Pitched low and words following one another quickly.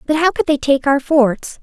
No: very high, 280 Hz; fast, 260 wpm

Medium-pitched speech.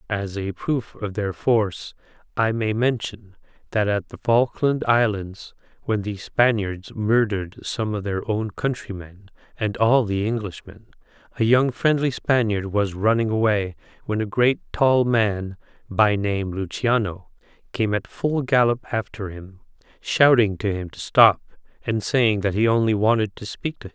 No: low, 110 Hz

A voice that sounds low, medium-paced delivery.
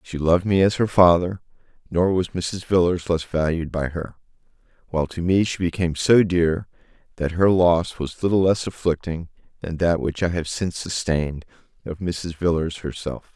Yes: very low, 85 Hz; average, 175 wpm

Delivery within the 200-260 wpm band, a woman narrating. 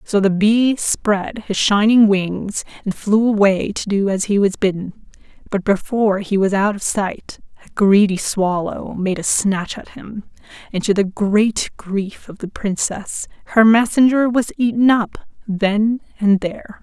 No: average, 170 wpm; female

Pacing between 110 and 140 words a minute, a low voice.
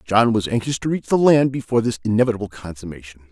No: average, 200 wpm; low, 110 Hz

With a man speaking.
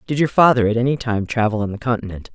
No: female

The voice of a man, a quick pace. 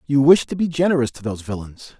Yes: male; fast, 240 wpm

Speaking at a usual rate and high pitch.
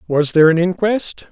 No: average, 185 wpm; medium, 175 Hz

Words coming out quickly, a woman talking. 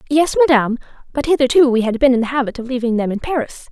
Yes: fast, 240 wpm; female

